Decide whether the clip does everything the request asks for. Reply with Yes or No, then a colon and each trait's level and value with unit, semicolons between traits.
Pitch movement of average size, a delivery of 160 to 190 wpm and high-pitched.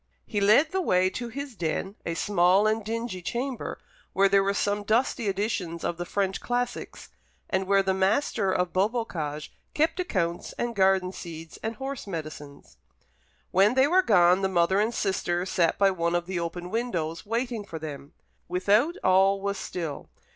Yes: average, 4.4 semitones; average, 170 wpm; high, 195 Hz